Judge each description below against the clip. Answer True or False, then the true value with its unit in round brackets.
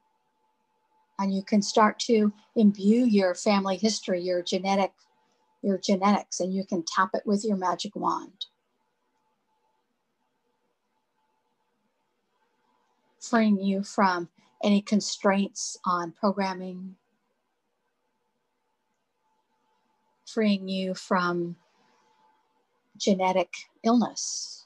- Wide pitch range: False (3.2 semitones)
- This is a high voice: True (200 Hz)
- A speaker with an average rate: False (85 wpm)